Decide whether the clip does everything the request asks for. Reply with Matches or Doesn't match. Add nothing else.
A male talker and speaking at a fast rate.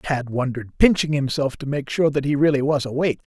Matches